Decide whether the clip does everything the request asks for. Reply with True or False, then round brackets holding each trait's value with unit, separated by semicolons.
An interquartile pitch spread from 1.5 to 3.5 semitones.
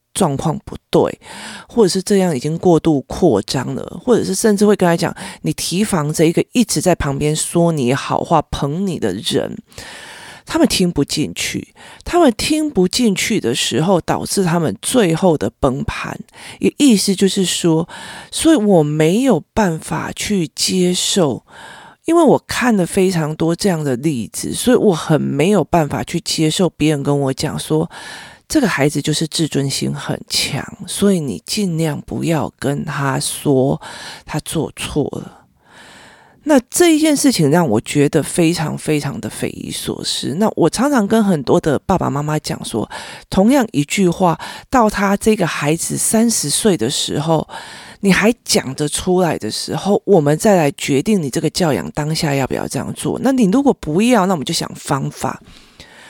False (5.3 semitones)